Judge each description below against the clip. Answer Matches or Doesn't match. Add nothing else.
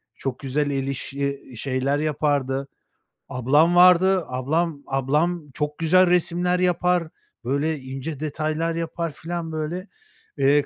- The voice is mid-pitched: Matches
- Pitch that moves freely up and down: Doesn't match